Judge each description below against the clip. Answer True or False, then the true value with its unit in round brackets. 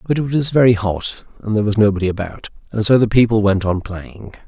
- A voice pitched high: False (105 Hz)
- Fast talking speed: True (230 wpm)